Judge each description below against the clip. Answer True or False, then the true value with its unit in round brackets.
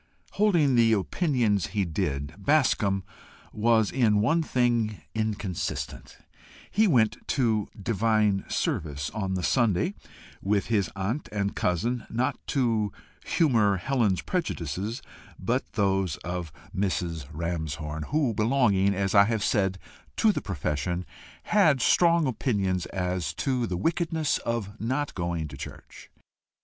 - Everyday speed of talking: False (125 wpm)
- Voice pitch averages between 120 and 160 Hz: False (105 Hz)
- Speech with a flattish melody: False (5.1 semitones)